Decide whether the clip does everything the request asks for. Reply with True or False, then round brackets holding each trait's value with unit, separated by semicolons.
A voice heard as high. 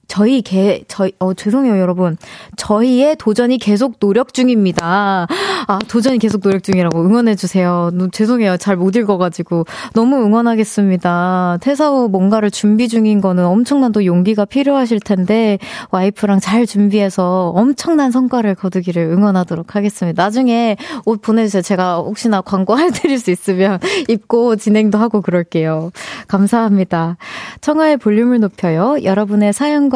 True (205 Hz)